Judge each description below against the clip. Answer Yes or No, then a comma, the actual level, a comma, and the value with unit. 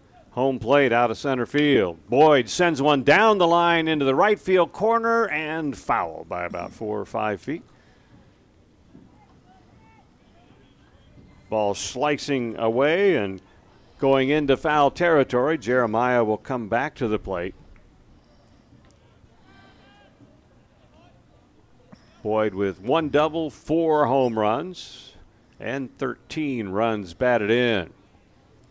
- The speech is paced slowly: Yes, slow, 110 wpm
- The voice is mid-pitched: No, low, 130 Hz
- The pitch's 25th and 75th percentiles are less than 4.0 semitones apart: No, average, 5.3 semitones